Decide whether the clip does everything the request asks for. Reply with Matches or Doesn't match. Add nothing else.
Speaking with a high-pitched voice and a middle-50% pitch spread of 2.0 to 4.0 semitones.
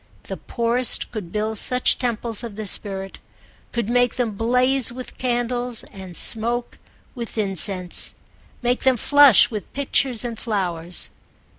Matches